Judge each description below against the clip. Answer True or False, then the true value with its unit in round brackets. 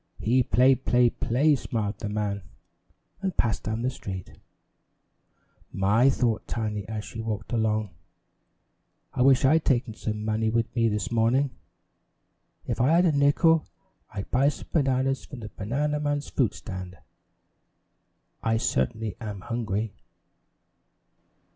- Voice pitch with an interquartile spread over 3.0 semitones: True (3.9 semitones)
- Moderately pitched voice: False (115 Hz)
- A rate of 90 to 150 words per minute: True (135 wpm)